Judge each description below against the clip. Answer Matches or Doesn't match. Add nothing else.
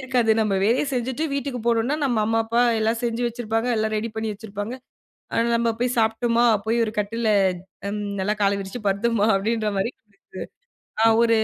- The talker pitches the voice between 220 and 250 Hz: Matches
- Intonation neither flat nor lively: Doesn't match